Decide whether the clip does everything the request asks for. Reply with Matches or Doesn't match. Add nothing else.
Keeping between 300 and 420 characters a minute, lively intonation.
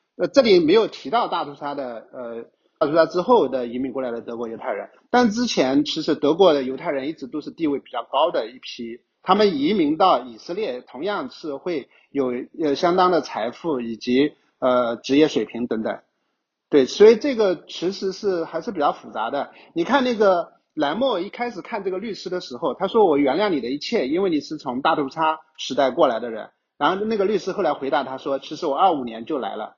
Matches